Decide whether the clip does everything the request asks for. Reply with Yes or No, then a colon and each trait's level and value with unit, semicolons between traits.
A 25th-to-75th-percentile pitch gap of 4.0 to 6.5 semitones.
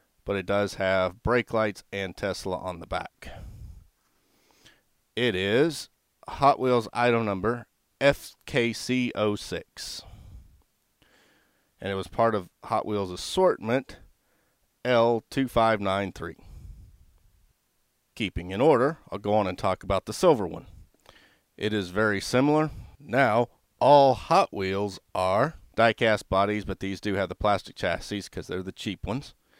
No: average, 3.5 semitones